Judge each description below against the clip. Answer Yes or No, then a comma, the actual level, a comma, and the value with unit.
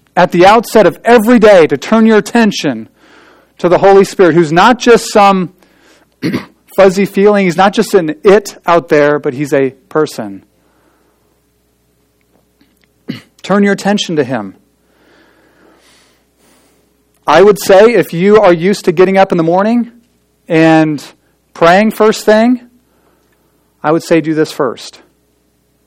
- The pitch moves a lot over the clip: Yes, wide, 6.0 semitones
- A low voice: No, medium, 175 Hz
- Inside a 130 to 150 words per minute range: Yes, slow, 135 wpm